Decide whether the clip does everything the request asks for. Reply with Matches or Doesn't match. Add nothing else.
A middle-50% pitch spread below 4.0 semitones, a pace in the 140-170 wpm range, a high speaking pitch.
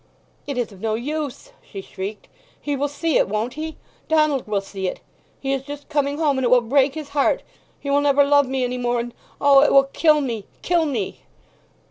Doesn't match